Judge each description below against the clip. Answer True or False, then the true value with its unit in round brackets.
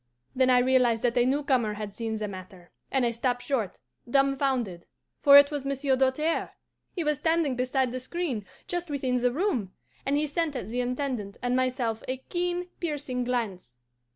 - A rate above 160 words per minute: True (180 wpm)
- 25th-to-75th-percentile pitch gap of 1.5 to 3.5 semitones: True (3.2 semitones)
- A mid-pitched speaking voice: False (255 Hz)